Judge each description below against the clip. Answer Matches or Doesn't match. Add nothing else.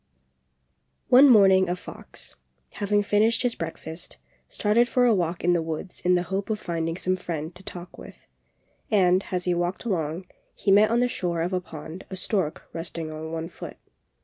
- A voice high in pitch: Doesn't match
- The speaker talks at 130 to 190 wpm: Matches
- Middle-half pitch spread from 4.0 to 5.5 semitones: Doesn't match